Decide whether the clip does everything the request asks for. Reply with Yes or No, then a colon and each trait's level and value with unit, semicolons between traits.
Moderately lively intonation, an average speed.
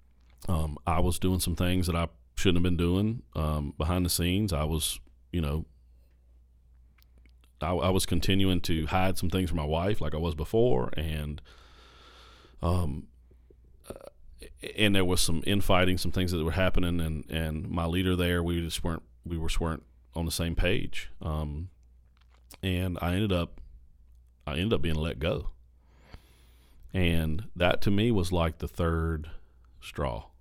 Yes: average, 4.8 semitones; average, 165 wpm